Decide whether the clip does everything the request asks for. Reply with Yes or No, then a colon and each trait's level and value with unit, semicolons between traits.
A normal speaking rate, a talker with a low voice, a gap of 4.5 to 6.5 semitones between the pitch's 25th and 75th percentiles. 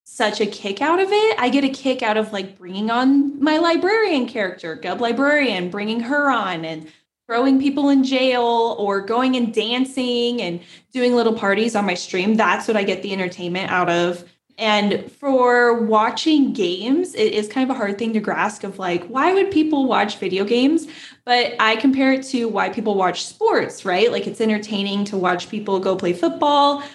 No: average, 195 wpm; high, 230 Hz; average, 5.3 semitones